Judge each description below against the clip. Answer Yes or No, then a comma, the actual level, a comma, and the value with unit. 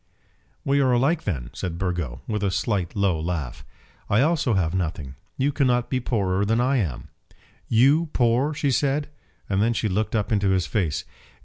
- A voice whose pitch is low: Yes, low, 105 Hz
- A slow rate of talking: No, average, 180 wpm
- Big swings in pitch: Yes, wide, 6.3 semitones